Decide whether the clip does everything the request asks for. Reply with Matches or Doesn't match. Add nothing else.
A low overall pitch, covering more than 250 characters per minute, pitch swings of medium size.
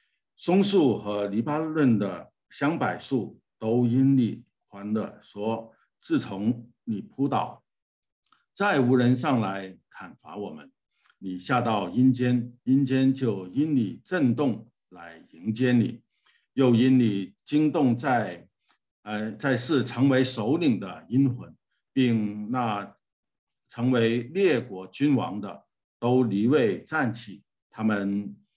Doesn't match